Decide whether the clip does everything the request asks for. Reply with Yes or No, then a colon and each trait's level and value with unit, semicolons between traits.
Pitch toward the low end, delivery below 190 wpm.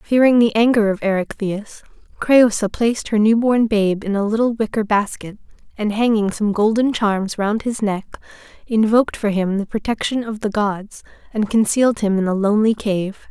No: high, 215 Hz; average, 175 wpm